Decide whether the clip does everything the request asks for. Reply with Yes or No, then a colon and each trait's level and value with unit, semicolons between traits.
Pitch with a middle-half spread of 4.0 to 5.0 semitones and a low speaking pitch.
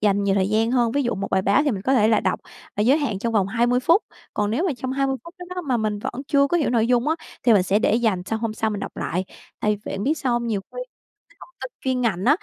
No: average, 4.4 semitones; high, 235 Hz